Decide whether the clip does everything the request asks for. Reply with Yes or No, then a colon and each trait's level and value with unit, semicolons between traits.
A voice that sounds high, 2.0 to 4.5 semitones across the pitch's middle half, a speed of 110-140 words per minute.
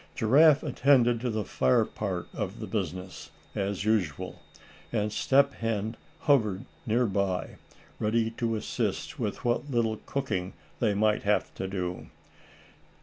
No: low, 110 Hz; average, 3.5 semitones; slow, 135 wpm